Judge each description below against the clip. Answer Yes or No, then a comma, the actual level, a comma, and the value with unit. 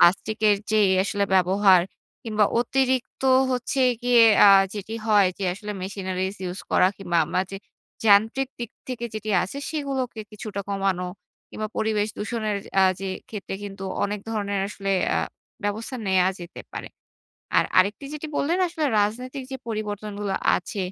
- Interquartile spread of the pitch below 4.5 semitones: Yes, average, 2.9 semitones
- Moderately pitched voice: No, high, 210 Hz